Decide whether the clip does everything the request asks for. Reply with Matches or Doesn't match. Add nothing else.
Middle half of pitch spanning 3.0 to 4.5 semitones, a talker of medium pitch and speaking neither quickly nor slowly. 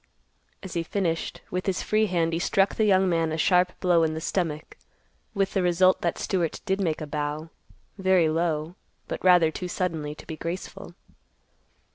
Doesn't match